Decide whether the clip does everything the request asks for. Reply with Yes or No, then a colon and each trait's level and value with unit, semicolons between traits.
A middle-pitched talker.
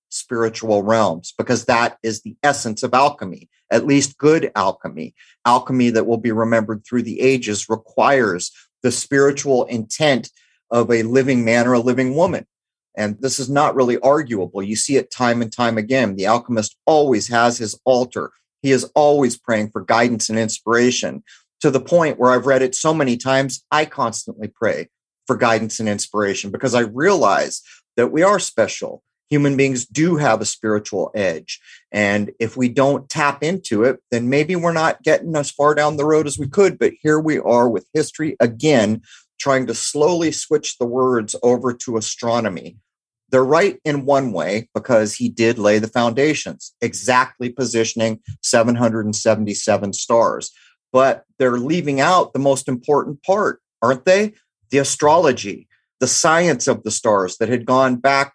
No: low, 125 Hz